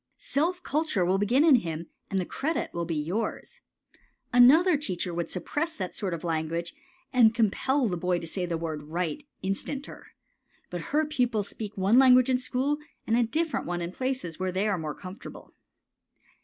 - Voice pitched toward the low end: No, high, 205 Hz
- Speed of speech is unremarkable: Yes, average, 180 wpm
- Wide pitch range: Yes, wide, 7.4 semitones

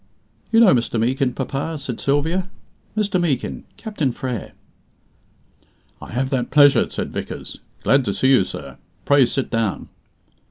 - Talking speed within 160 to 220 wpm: No, average, 145 wpm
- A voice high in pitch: No, low, 135 Hz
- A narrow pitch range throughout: No, average, 4.2 semitones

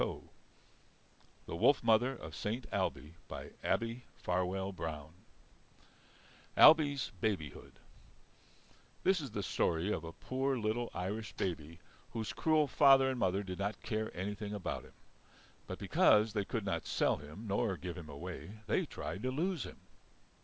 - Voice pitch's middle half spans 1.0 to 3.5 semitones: No, average, 5.3 semitones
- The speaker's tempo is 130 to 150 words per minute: Yes, average, 140 wpm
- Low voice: Yes, low, 105 Hz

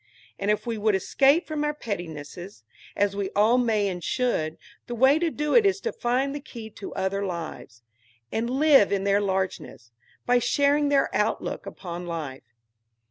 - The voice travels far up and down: Yes, wide, 6.3 semitones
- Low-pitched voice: No, high, 210 Hz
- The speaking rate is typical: Yes, average, 175 wpm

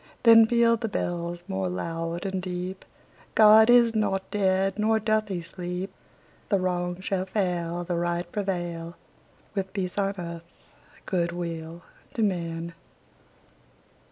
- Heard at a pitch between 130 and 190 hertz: Yes, medium, 185 Hz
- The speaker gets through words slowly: Yes, slow, 130 wpm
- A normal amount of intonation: Yes, average, 3.0 semitones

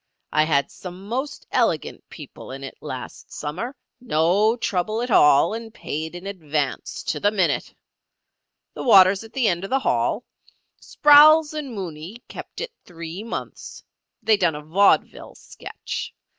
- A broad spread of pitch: Yes, wide, 6.4 semitones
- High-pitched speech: Yes, high, 195 Hz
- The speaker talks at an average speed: Yes, average, 145 wpm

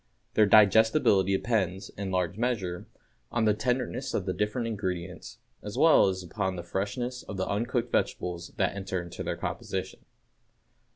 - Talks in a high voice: No, low, 100 Hz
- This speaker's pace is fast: No, average, 155 wpm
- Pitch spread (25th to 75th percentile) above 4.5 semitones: No, average, 3.8 semitones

